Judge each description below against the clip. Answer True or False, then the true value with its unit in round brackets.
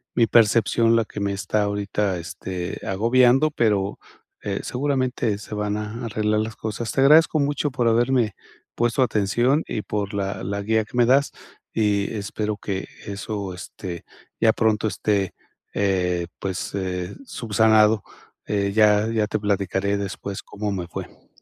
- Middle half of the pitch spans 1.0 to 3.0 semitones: True (2.6 semitones)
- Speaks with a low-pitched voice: True (105 Hz)